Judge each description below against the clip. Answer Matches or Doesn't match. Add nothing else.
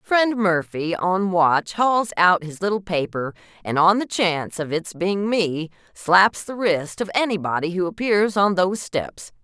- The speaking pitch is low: Doesn't match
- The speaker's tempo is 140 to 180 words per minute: Matches